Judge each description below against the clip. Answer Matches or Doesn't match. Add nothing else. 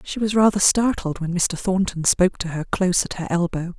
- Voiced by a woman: Matches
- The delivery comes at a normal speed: Doesn't match